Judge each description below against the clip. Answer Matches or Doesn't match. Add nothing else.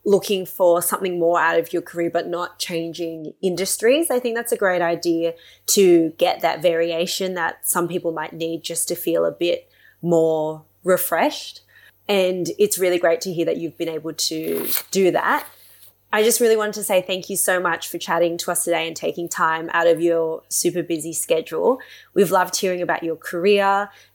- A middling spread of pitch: Doesn't match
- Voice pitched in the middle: Matches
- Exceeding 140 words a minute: Matches